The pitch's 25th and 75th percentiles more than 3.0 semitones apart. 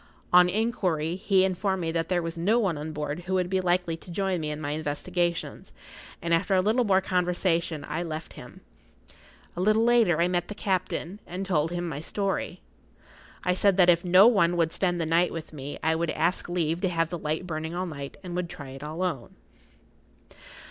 No: narrow, 2.5 semitones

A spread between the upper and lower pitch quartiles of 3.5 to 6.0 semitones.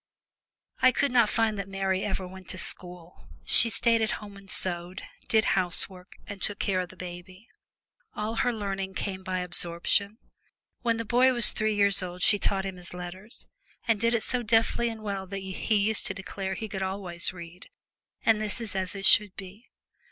No: average, 2.9 semitones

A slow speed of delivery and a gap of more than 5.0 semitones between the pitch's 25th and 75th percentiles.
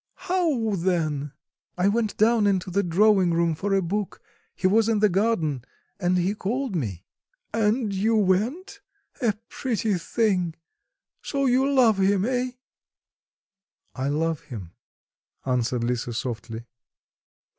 Yes: slow, 130 wpm; wide, 5.6 semitones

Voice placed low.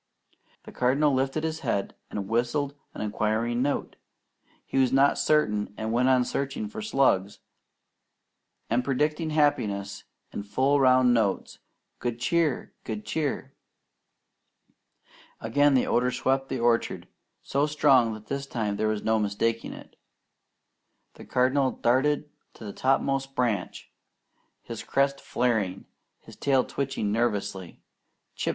Yes: low, 125 Hz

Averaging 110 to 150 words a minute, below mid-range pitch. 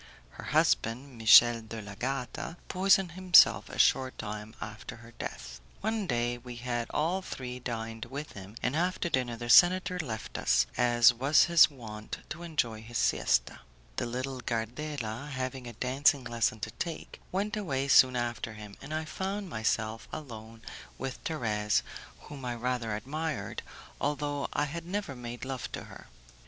No: average, 160 wpm; low, 125 Hz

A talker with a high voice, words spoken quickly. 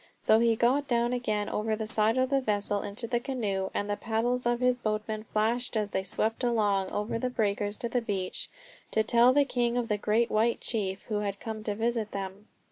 Yes: high, 220 Hz; fast, 215 wpm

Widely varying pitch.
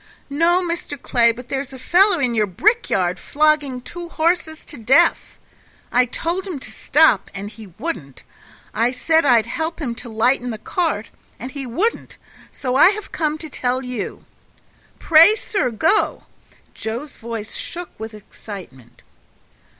Yes: wide, 6.4 semitones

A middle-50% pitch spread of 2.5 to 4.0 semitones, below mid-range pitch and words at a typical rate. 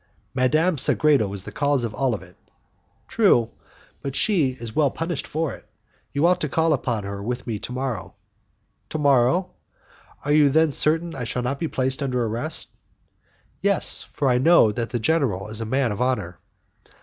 No: average, 4.6 semitones; low, 130 Hz; average, 185 wpm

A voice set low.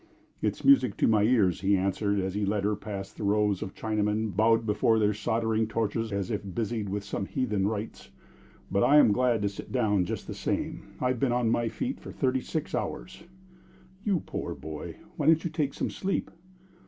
Yes: low, 110 Hz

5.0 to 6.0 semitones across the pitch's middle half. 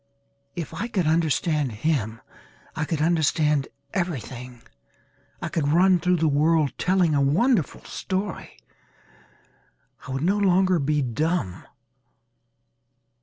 No: average, 4.2 semitones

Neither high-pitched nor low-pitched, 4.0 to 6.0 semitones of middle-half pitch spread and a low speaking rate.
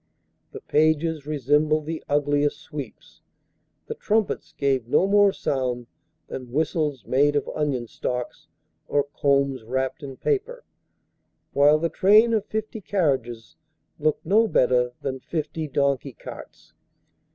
No: medium, 145 Hz; average, 3.5 semitones; slow, 125 wpm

